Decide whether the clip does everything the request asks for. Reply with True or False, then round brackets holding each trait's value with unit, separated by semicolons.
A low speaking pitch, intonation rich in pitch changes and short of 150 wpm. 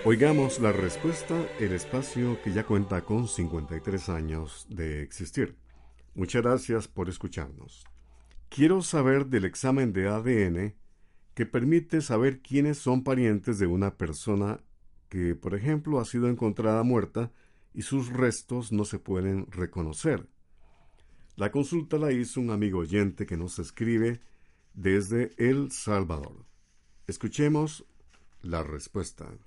True (105 Hz; 6.2 semitones; 125 wpm)